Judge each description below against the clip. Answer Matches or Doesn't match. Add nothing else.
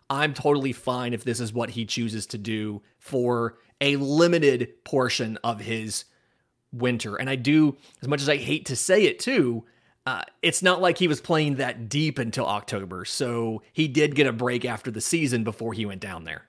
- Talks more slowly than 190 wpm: Doesn't match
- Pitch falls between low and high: Doesn't match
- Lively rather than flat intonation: Doesn't match